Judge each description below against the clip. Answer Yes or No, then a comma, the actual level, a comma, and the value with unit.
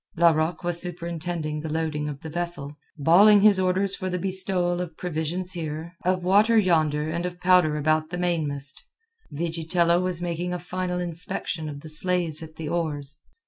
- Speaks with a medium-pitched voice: Yes, medium, 170 Hz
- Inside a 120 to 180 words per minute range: Yes, average, 170 wpm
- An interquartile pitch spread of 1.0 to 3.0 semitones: Yes, narrow, 2.4 semitones